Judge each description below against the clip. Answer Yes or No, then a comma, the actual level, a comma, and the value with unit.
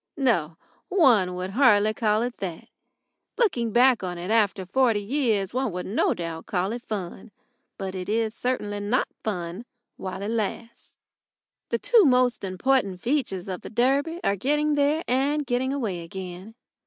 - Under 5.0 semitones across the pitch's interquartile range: No, wide, 5.4 semitones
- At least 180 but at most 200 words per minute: No, average, 160 wpm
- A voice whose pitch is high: Yes, high, 220 Hz